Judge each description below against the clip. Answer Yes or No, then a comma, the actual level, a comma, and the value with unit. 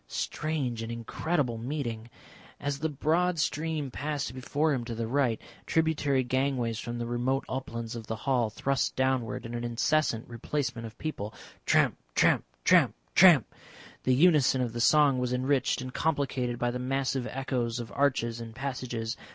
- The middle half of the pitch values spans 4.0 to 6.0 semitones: No, average, 3.2 semitones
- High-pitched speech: No, low, 130 Hz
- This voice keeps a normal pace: Yes, average, 160 wpm